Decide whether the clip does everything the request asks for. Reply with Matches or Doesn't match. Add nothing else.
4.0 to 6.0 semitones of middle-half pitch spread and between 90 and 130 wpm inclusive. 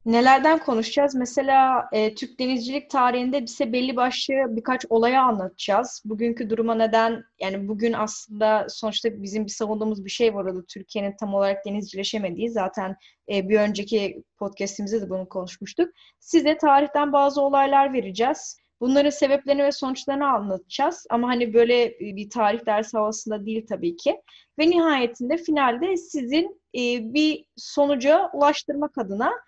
Doesn't match